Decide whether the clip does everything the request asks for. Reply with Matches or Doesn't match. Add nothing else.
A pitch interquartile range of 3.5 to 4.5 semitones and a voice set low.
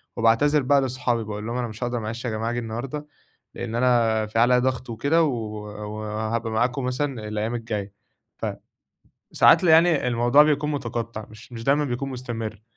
Doesn't match